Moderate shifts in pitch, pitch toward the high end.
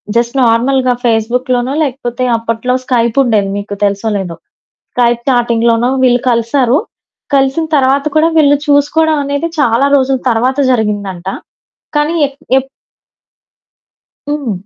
Yes: average, 3.1 semitones; high, 245 Hz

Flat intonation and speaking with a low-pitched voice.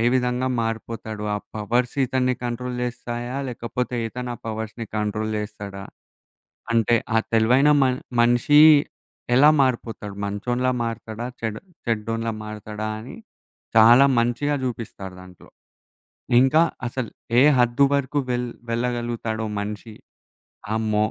Yes: narrow, 2.2 semitones; low, 115 Hz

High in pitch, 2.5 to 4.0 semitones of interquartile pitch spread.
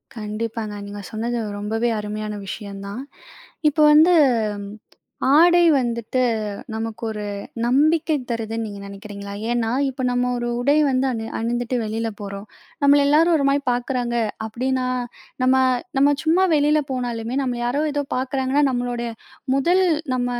Yes: high, 245 Hz; average, 3.7 semitones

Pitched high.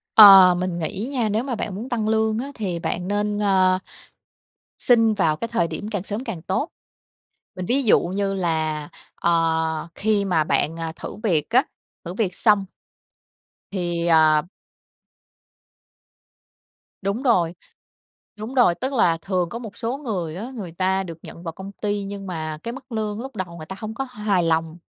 Yes: high, 195 Hz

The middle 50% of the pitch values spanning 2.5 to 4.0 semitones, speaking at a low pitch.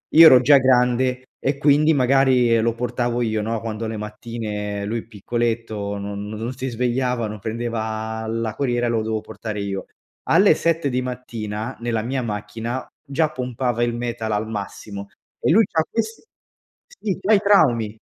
Yes: average, 2.9 semitones; low, 120 Hz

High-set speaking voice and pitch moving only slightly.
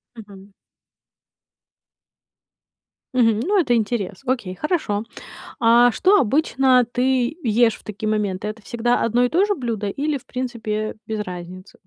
No: high, 230 Hz; average, 3.4 semitones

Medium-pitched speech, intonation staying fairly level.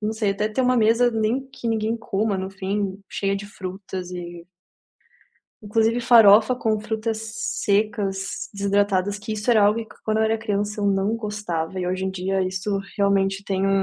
No: high, 205 Hz; narrow, 2.2 semitones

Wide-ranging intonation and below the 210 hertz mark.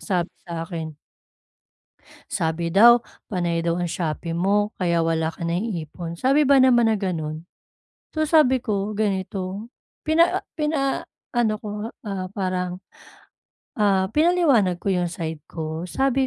Yes: wide, 5.8 semitones; high, 190 Hz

